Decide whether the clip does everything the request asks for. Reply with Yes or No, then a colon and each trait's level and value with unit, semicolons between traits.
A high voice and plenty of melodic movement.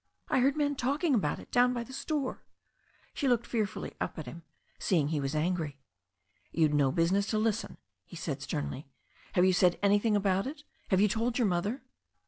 Yes: high, 200 Hz; wide, 6.7 semitones